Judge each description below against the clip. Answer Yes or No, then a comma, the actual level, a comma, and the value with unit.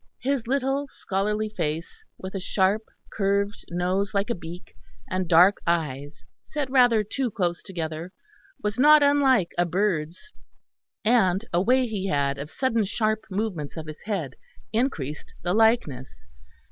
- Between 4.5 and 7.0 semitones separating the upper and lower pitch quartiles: Yes, average, 5.1 semitones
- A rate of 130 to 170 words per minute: Yes, average, 145 wpm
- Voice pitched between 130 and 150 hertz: No, high, 200 Hz